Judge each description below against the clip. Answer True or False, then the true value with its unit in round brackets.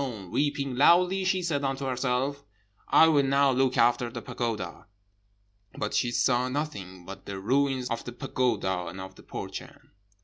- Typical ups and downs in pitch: True (3.4 semitones)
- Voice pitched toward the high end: False (130 Hz)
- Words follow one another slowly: False (160 wpm)